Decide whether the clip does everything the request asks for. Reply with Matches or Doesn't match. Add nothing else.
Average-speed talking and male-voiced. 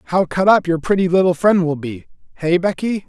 Doesn't match